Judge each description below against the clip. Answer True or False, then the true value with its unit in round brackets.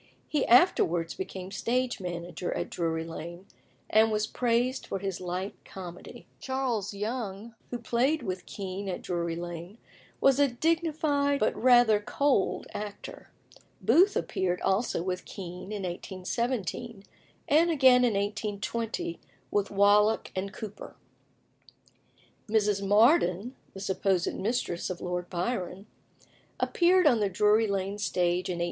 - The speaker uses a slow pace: True (130 wpm)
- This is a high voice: True (205 Hz)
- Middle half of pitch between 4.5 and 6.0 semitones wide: True (4.8 semitones)